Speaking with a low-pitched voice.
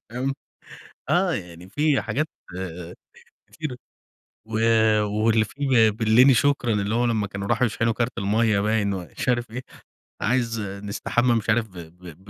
Yes: low, 110 Hz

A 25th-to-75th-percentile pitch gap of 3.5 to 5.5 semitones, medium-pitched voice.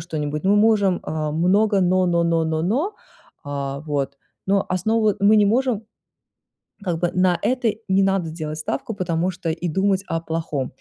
Yes: average, 4.0 semitones; medium, 180 Hz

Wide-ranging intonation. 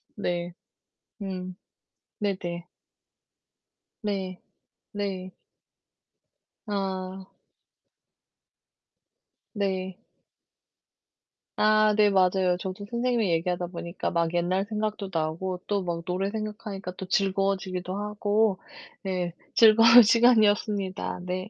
No: narrow, 2.3 semitones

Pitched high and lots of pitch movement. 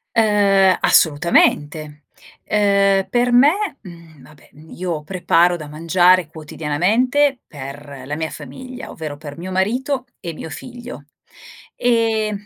No: medium, 180 Hz; wide, 6.0 semitones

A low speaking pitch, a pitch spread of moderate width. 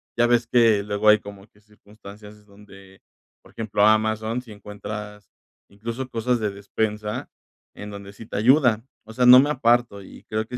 No: low, 105 Hz; narrow, 2.3 semitones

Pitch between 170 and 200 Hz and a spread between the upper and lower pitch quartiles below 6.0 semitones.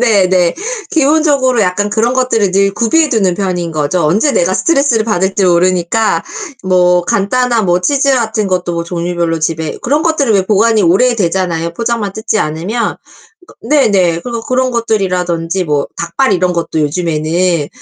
Yes: high, 190 Hz; average, 5.1 semitones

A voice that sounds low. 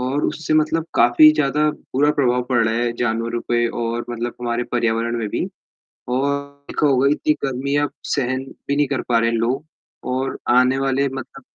Yes: low, 130 Hz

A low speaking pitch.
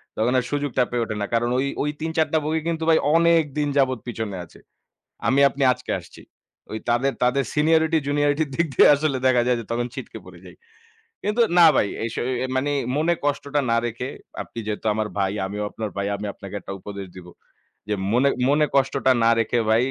Yes: low, 130 Hz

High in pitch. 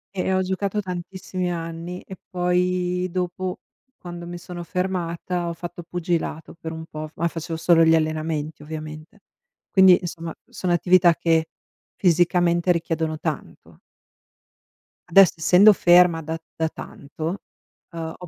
No: medium, 175 Hz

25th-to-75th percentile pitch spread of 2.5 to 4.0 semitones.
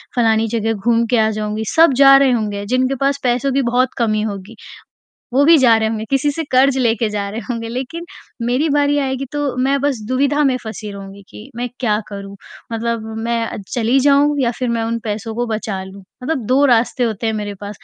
Yes: average, 3.6 semitones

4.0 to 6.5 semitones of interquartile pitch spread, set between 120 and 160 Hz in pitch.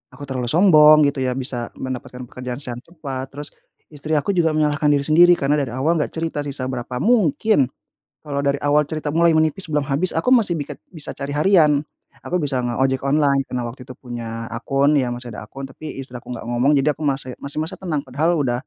No: average, 3.2 semitones; medium, 140 Hz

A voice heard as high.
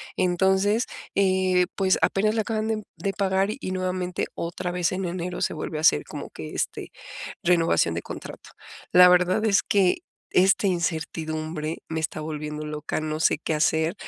No: medium, 180 Hz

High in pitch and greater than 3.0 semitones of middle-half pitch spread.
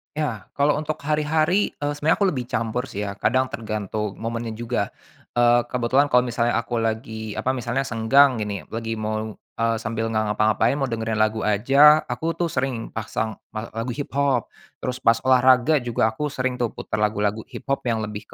No: low, 120 Hz; average, 3.6 semitones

